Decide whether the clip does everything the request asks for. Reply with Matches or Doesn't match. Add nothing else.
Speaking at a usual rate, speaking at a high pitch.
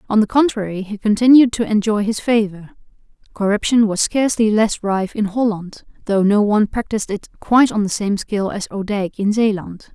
Matches